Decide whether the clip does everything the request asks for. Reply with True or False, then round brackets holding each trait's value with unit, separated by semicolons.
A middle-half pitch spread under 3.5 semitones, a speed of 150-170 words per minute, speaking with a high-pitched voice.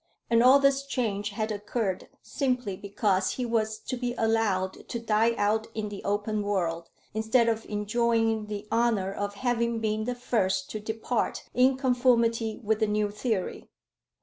True (2.4 semitones; 160 wpm; 220 Hz)